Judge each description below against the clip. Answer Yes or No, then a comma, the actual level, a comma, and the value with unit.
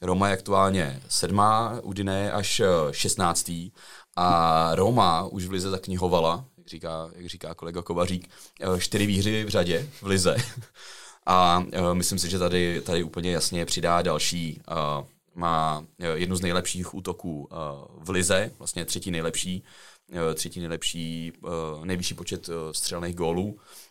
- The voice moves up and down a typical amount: No, narrow, 2.3 semitones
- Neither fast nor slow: Yes, average, 130 wpm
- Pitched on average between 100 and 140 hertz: No, very low, 90 Hz